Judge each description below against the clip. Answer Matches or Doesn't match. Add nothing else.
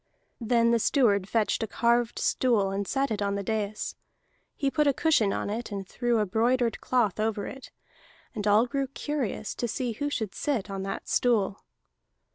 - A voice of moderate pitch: Doesn't match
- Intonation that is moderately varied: Matches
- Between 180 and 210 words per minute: Matches